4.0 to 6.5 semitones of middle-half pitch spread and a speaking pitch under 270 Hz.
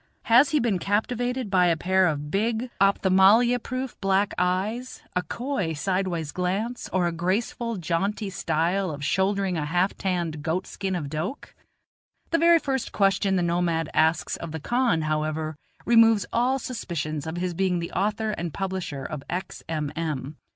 Yes: average, 5.0 semitones; medium, 185 Hz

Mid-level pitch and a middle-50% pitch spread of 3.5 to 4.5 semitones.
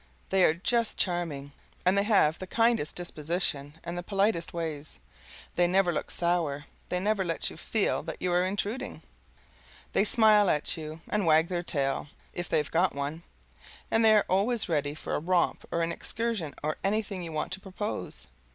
Yes: medium, 175 Hz; average, 4.2 semitones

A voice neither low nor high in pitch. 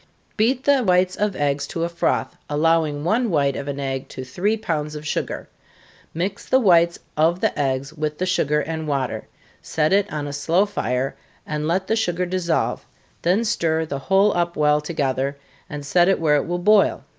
Yes: medium, 165 Hz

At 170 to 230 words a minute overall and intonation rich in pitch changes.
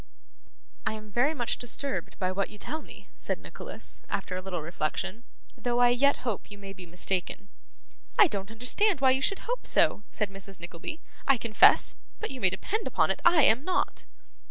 Yes: average, 190 wpm; wide, 6.3 semitones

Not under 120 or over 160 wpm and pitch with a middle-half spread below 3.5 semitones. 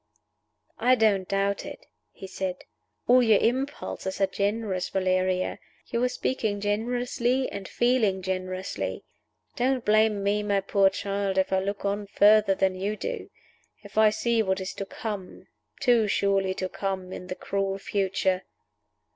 Yes: average, 150 wpm; narrow, 2.5 semitones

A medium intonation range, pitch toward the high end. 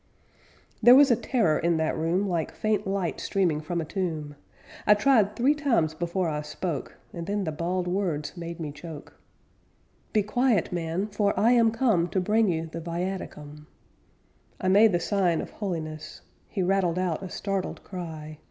No: average, 4.0 semitones; medium, 180 Hz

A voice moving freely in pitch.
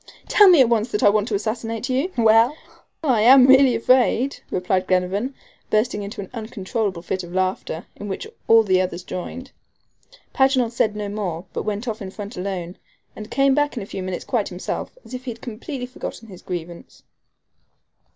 No: average, 4.9 semitones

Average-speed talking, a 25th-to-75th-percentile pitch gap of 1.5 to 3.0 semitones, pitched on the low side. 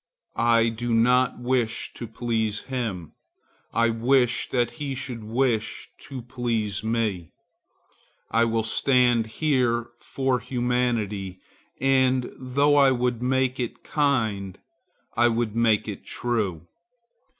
No: slow, 115 wpm; narrow, 2.4 semitones; low, 120 Hz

